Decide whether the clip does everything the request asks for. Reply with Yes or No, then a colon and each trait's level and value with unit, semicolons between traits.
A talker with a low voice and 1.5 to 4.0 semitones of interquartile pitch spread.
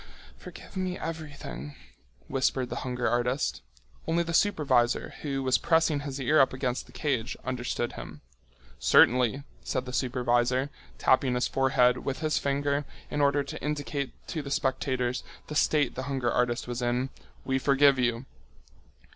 Yes: low, 130 Hz; narrow, 2.6 semitones